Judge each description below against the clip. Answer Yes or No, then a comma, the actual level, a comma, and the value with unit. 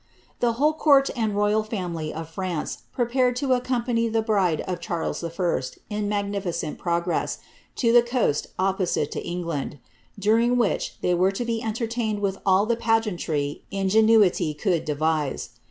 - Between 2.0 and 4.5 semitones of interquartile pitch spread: No, average, 5.0 semitones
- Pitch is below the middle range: No, high, 205 Hz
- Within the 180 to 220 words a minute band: No, average, 155 wpm